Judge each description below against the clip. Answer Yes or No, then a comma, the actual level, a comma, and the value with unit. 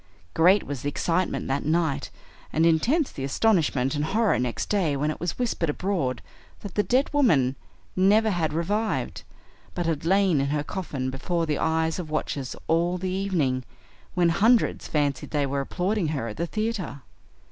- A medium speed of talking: Yes, average, 170 wpm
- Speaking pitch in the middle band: Yes, medium, 165 Hz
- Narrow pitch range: No, average, 5.2 semitones